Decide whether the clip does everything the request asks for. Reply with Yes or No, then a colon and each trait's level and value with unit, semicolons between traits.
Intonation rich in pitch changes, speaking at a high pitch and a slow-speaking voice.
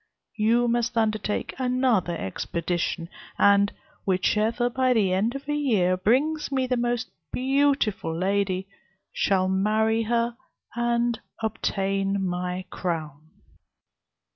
No: average, 4.4 semitones; high, 215 Hz; slow, 110 wpm